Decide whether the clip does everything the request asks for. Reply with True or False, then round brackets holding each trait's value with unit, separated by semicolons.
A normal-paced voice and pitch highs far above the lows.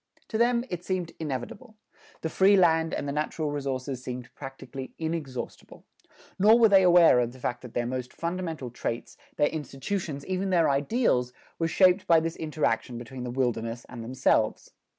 True (170 wpm; 5.9 semitones)